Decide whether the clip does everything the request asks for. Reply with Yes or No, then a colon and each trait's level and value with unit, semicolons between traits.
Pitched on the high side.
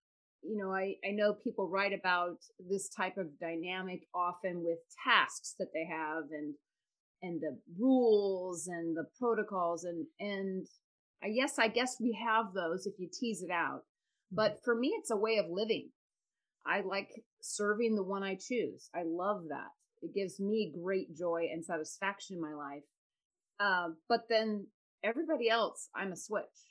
Yes: high, 195 Hz